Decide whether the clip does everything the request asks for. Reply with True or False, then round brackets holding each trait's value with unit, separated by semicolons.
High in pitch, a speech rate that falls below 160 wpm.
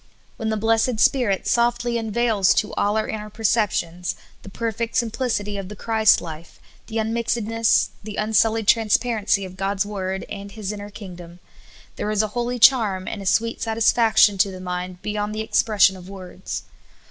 False (210 Hz; 170 wpm)